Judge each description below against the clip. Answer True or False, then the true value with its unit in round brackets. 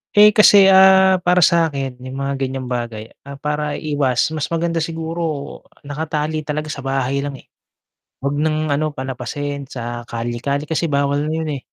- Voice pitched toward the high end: False (145 Hz)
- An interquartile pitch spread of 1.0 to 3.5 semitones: True (3.1 semitones)